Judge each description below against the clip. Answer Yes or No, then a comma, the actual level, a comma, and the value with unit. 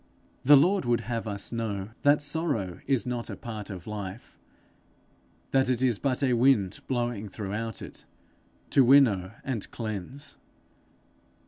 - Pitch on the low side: Yes, low, 115 Hz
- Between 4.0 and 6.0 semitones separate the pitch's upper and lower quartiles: Yes, average, 4.3 semitones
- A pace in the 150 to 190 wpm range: No, average, 140 wpm